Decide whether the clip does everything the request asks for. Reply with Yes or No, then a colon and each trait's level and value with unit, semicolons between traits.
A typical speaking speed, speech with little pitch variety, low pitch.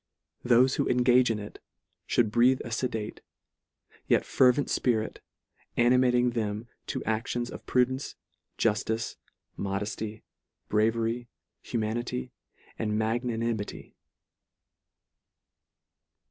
No: slow, 90 wpm; narrow, 2.2 semitones; low, 115 Hz